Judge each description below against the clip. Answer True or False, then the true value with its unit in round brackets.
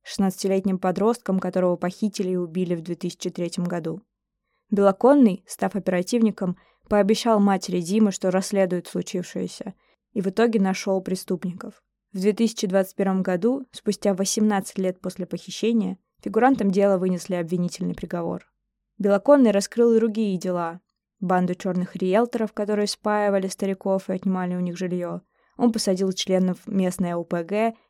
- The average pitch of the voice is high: True (195 Hz)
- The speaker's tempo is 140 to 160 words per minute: False (125 wpm)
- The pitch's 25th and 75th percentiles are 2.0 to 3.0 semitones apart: True (2.6 semitones)